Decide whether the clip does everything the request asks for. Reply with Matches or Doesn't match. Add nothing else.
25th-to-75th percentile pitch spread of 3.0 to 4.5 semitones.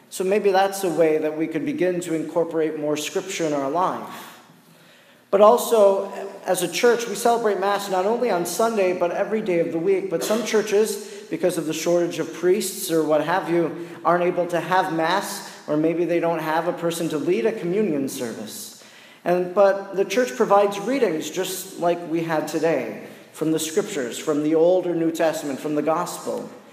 Matches